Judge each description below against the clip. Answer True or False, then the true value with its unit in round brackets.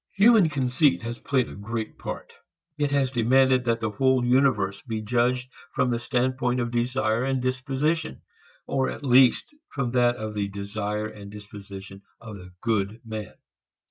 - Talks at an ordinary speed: True (160 wpm)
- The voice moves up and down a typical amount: True (3.4 semitones)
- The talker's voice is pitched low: True (120 Hz)